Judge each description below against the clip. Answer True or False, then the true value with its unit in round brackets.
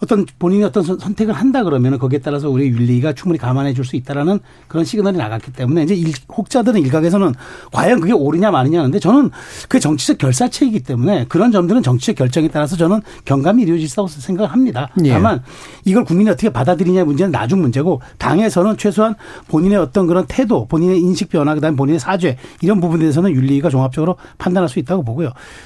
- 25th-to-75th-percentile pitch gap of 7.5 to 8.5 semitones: False (5.7 semitones)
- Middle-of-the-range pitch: True (175 Hz)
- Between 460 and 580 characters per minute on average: True (480 characters per minute)